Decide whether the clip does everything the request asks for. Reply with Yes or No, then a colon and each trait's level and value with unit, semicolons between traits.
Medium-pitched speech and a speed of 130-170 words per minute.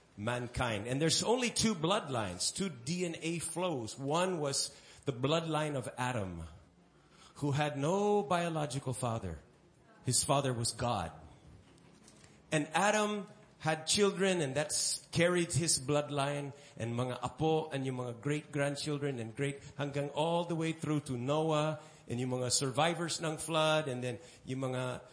Yes: medium, 145 Hz; average, 140 wpm